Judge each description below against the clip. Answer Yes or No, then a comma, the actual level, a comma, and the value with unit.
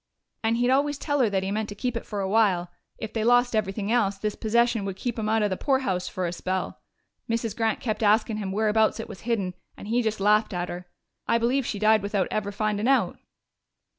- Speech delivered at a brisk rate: Yes, fast, 230 wpm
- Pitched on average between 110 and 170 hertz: No, high, 215 Hz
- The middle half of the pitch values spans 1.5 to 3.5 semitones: Yes, average, 2.7 semitones